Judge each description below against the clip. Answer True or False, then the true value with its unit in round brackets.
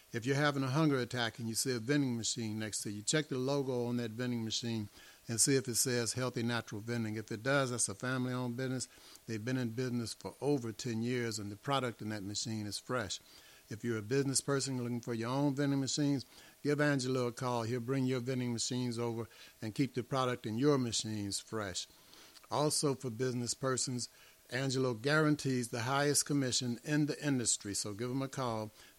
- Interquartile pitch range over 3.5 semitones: False (2.9 semitones)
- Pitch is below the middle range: True (125 Hz)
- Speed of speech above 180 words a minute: True (205 wpm)